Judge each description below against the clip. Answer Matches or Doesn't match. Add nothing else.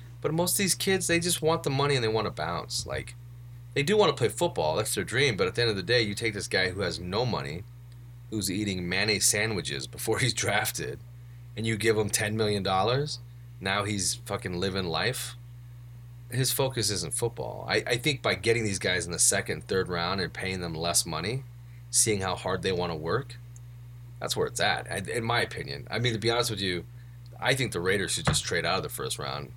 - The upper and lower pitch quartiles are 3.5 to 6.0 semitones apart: Doesn't match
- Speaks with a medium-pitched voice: Doesn't match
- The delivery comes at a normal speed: Doesn't match